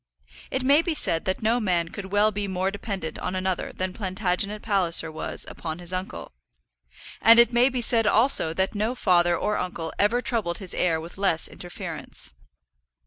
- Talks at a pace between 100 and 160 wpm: No, average, 180 wpm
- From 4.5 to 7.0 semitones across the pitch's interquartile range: No, average, 3.9 semitones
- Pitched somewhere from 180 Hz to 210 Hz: Yes, high, 190 Hz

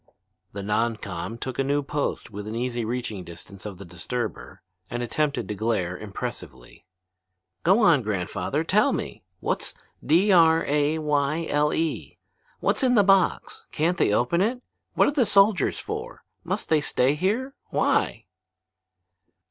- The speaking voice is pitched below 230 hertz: Yes, medium, 140 Hz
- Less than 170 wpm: Yes, average, 150 wpm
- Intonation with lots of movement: Yes, wide, 8.0 semitones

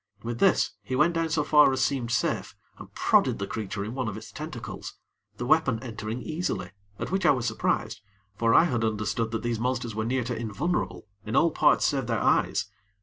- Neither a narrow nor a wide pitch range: Yes, average, 4.4 semitones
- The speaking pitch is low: Yes, low, 120 Hz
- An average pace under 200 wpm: No, fast, 205 wpm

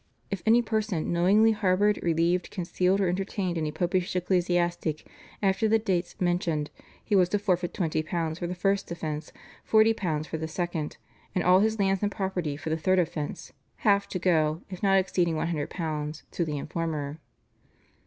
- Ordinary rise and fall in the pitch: Yes, average, 3.2 semitones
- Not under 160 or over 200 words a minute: Yes, average, 165 wpm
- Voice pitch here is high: No, medium, 175 Hz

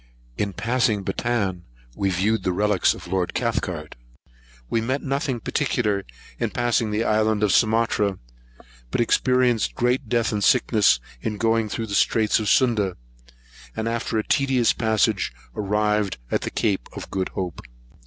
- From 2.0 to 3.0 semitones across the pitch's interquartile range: Yes, average, 2.7 semitones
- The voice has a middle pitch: No, low, 110 Hz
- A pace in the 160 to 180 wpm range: No, average, 150 wpm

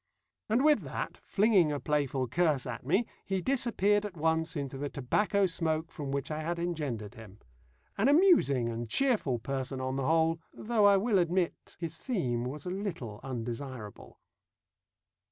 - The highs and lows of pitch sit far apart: Yes, wide, 7.0 semitones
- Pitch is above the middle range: No, medium, 160 Hz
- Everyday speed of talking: Yes, average, 160 wpm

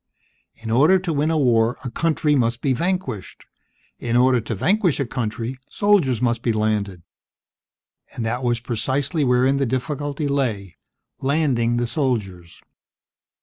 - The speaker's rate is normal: Yes, average, 145 wpm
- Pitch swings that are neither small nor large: Yes, average, 4.0 semitones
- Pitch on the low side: Yes, low, 125 Hz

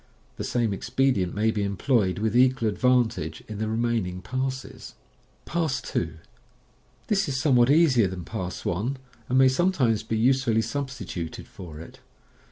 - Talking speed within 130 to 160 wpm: Yes, average, 155 wpm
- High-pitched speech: No, low, 115 Hz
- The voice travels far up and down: No, average, 4.7 semitones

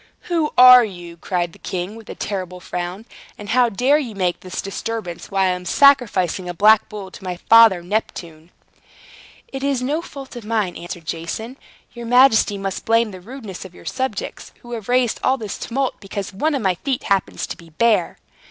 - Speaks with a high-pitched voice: Yes, high, 210 Hz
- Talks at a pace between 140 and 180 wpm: No, average, 195 wpm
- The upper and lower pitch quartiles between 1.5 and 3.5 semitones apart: No, average, 5.3 semitones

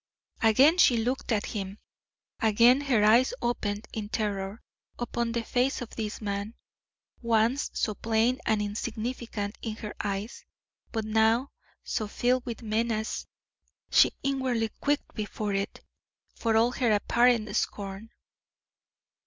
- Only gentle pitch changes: Yes, narrow, 2.3 semitones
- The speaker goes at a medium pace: No, slow, 130 wpm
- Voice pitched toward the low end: No, high, 225 Hz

